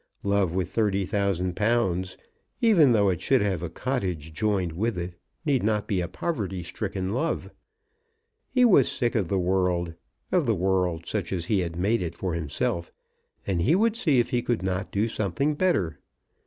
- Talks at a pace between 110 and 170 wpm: No, average, 180 wpm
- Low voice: Yes, very low, 95 Hz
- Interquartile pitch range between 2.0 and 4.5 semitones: No, average, 4.9 semitones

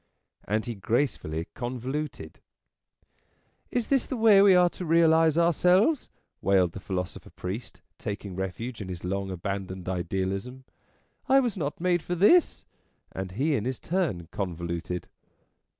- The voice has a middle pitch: No, low, 120 Hz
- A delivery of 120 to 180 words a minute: Yes, average, 150 wpm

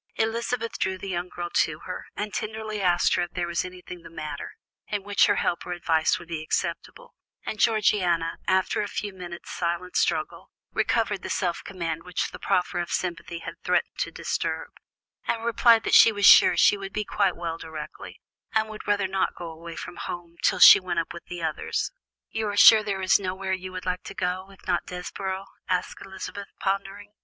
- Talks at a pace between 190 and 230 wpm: Yes, average, 195 wpm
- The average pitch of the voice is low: No, medium, 185 Hz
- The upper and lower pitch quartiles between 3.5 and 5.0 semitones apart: No, average, 2.9 semitones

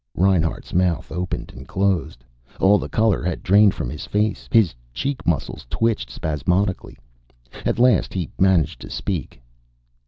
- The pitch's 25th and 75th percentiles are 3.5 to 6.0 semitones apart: Yes, average, 4.3 semitones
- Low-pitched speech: Yes, very low, 90 Hz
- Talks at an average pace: Yes, average, 145 wpm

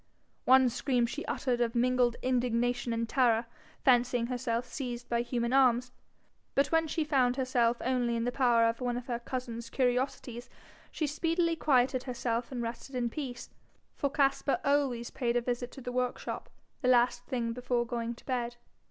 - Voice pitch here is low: No, high, 245 Hz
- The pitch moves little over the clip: Yes, narrow, 1.6 semitones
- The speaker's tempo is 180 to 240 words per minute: No, average, 170 wpm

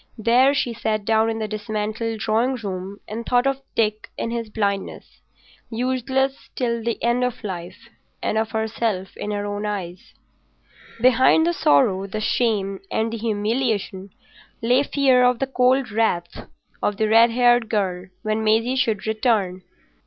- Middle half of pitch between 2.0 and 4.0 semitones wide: Yes, average, 2.8 semitones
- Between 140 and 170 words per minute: Yes, average, 155 wpm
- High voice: Yes, high, 220 Hz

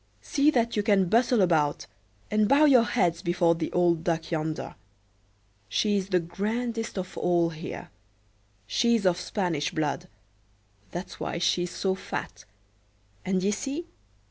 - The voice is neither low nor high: Yes, medium, 180 Hz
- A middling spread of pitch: Yes, average, 4.5 semitones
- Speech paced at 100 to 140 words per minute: Yes, slow, 135 wpm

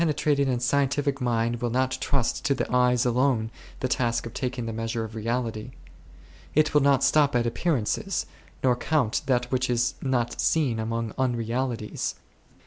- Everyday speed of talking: Yes, average, 165 wpm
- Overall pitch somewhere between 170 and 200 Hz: No, low, 125 Hz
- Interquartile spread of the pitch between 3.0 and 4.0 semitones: No, narrow, 2.6 semitones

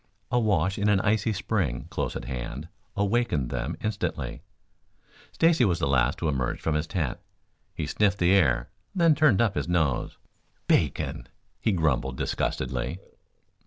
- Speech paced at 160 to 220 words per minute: No, average, 150 wpm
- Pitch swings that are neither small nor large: No, wide, 7.6 semitones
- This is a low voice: Yes, very low, 90 Hz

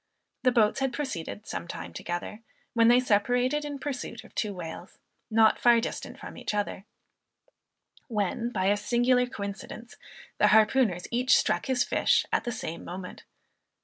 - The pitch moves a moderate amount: Yes, average, 3.4 semitones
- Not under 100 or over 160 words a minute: Yes, average, 155 wpm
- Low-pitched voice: No, high, 230 Hz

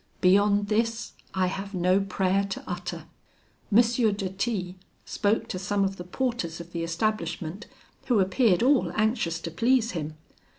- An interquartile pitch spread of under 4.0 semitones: Yes, average, 3.4 semitones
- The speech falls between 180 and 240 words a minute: No, average, 155 wpm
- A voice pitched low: No, high, 195 Hz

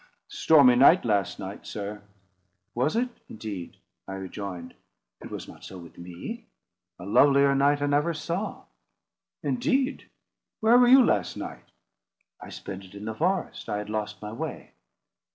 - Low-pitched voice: Yes, low, 115 Hz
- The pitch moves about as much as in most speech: No, wide, 8.3 semitones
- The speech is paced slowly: No, average, 150 wpm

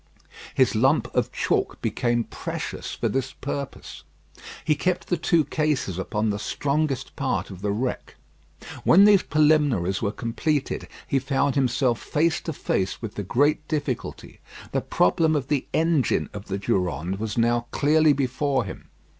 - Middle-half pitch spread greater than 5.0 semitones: Yes, wide, 5.6 semitones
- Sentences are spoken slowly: No, average, 155 wpm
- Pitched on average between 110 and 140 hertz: Yes, low, 135 Hz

